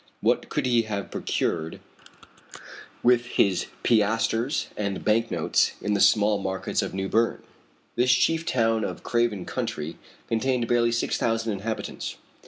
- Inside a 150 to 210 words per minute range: No, average, 140 wpm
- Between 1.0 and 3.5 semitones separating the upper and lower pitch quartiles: Yes, average, 2.8 semitones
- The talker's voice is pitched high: No, low, 115 Hz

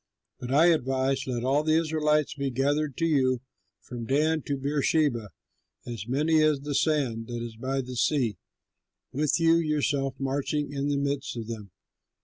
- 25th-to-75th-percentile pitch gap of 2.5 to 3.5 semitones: Yes, average, 3.0 semitones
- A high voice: No, medium, 140 Hz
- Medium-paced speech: Yes, average, 165 wpm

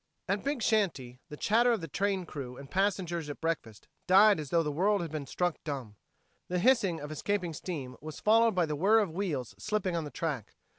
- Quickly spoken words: Yes, fast, 210 wpm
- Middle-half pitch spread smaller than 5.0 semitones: No, average, 5.3 semitones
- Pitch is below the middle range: No, medium, 175 Hz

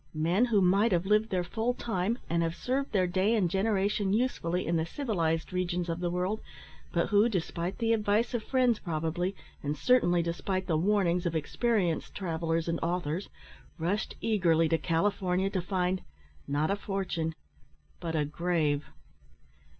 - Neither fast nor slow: Yes, average, 160 wpm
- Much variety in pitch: No, average, 3.7 semitones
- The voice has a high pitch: No, medium, 180 Hz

